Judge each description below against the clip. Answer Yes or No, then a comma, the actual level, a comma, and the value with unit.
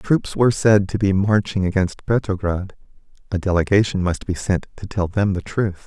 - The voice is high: No, low, 100 Hz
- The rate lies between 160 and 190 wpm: Yes, average, 175 wpm